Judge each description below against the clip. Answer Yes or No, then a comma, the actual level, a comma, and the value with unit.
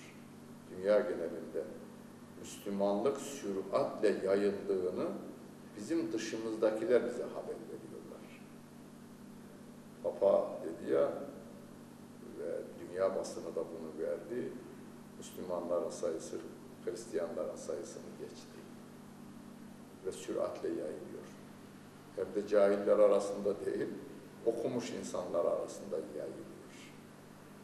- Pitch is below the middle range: No, high, 225 Hz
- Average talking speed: No, slow, 80 wpm